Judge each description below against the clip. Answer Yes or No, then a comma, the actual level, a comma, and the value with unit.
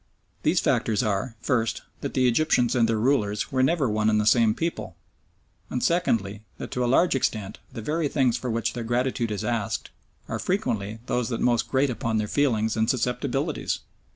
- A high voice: No, low, 120 Hz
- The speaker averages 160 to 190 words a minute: Yes, average, 185 wpm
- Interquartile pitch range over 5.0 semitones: No, average, 3.0 semitones